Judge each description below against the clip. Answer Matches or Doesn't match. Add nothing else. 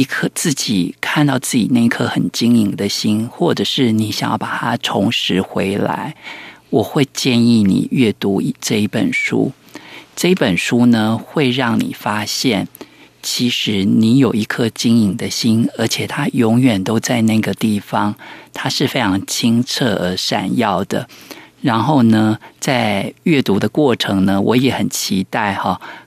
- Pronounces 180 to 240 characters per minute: Matches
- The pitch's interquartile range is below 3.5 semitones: Matches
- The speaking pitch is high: Doesn't match